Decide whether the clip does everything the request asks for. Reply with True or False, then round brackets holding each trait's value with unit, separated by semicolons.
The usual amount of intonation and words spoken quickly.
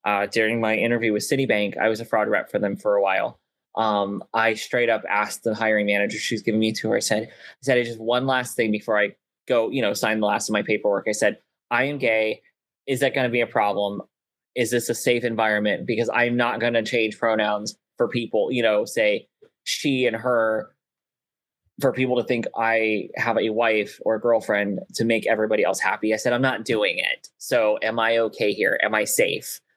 False (2.3 semitones; 225 wpm)